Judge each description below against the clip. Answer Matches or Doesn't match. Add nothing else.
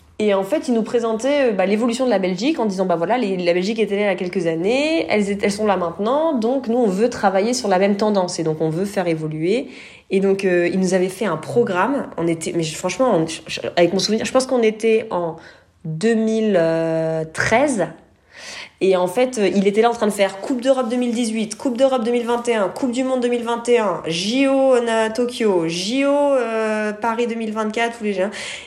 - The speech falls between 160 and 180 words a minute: Doesn't match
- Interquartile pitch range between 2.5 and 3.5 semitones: Doesn't match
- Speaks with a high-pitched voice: Matches